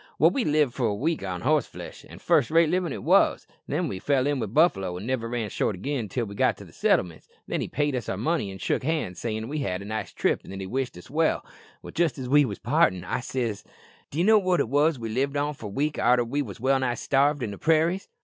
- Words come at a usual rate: No, fast, 265 wpm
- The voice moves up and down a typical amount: No, wide, 5.7 semitones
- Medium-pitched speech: No, low, 130 Hz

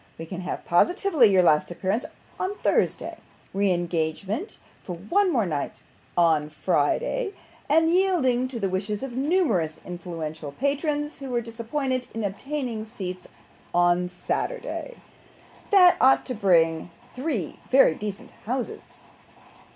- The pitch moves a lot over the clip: Yes, wide, 8.6 semitones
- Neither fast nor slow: No, slow, 130 wpm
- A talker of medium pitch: No, high, 220 Hz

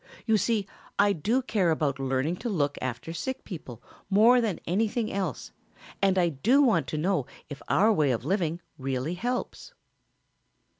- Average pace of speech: Yes, average, 160 wpm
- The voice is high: No, medium, 180 Hz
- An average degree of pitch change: No, wide, 7.1 semitones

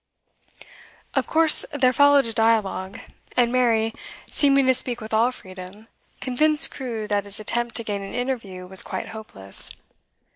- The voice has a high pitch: Yes, high, 230 Hz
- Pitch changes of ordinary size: Yes, average, 3.8 semitones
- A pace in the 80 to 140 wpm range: No, average, 150 wpm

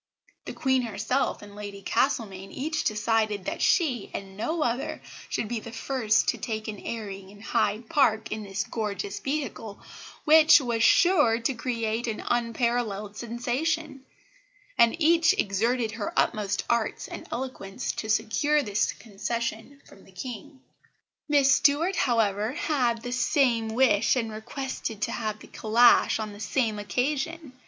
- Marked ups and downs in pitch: No, average, 3.9 semitones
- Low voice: No, high, 230 Hz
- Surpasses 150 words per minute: No, average, 145 wpm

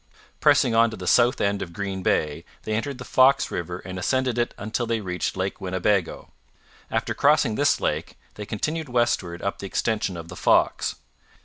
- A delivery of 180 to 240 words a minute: Yes, average, 185 wpm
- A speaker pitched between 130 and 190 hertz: No, low, 105 Hz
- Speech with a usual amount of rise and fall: Yes, average, 4.4 semitones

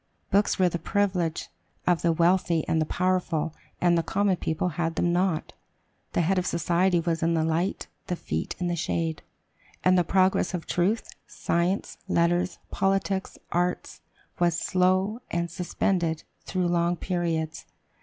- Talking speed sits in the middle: Yes, average, 155 wpm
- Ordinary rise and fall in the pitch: No, narrow, 1.8 semitones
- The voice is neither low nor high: Yes, medium, 175 Hz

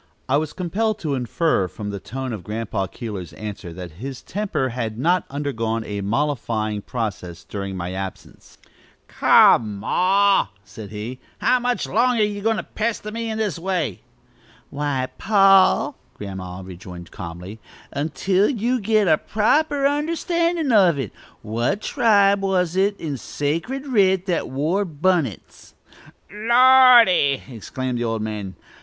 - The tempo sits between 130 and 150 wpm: Yes, average, 140 wpm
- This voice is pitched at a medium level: Yes, medium, 145 Hz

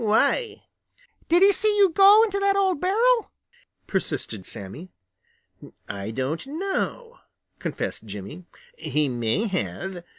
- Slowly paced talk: Yes, slow, 120 wpm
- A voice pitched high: Yes, high, 225 Hz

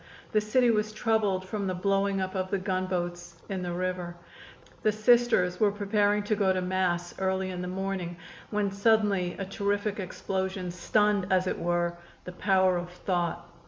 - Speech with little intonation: Yes, narrow, 2.2 semitones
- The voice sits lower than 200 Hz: Yes, high, 190 Hz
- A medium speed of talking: Yes, average, 170 wpm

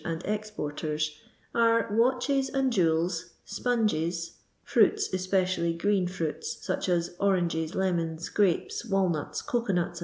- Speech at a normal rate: No, slow, 120 wpm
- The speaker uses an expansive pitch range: No, average, 4.4 semitones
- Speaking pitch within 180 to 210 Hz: Yes, medium, 185 Hz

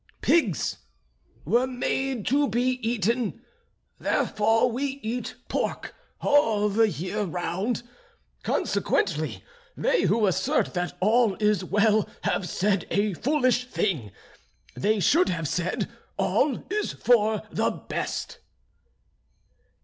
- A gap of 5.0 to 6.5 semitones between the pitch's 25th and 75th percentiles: No, average, 4.0 semitones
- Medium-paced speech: No, slow, 110 wpm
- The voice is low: No, high, 220 Hz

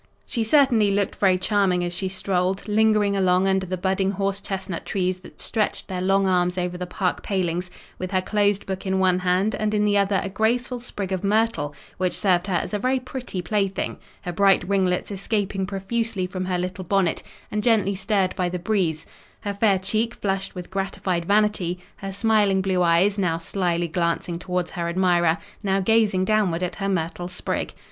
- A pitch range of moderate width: No, narrow, 2.1 semitones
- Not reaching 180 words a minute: No, average, 190 wpm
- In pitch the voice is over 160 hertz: Yes, high, 190 Hz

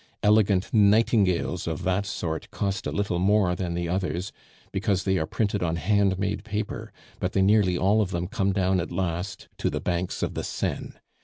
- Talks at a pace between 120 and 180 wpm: No, average, 190 wpm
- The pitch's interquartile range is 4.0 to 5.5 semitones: No, narrow, 2.4 semitones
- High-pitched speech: No, very low, 95 Hz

